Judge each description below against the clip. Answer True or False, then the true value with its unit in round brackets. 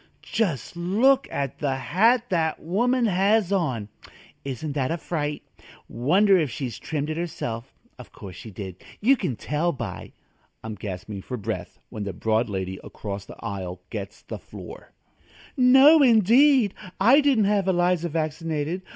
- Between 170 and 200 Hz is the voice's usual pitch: False (160 Hz)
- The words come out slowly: False (155 wpm)